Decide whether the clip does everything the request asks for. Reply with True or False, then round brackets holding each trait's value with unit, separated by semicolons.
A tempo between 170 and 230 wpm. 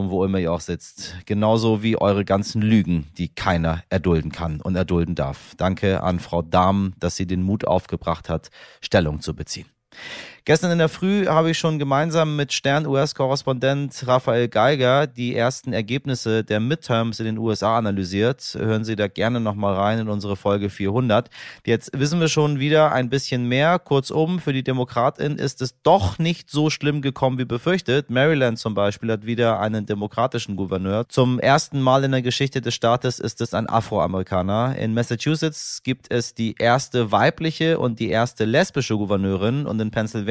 True (175 wpm)